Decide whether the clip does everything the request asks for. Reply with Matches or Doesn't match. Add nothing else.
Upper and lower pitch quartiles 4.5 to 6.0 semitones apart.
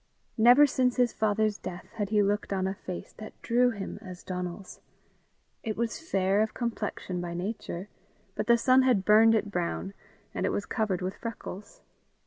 Doesn't match